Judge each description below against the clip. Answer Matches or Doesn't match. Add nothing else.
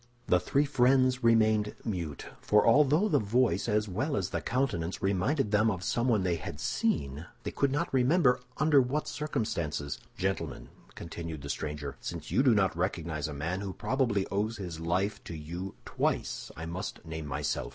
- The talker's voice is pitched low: Matches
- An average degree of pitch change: Doesn't match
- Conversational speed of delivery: Matches